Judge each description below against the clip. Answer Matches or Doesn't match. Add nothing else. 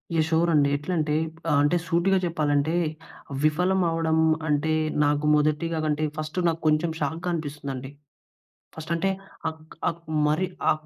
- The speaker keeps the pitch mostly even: Matches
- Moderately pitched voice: Matches